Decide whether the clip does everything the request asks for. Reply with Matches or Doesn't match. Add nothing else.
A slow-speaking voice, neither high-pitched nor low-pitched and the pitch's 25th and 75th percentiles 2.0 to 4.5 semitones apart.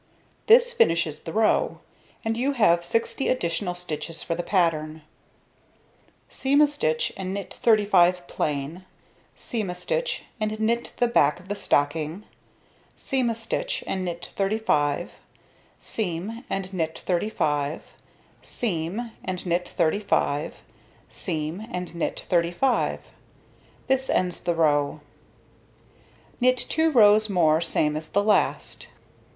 Doesn't match